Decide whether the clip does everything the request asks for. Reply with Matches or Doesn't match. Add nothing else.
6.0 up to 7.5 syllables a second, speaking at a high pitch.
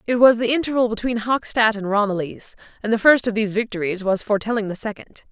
Matches